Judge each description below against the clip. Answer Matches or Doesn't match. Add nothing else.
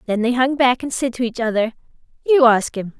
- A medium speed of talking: Doesn't match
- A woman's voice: Matches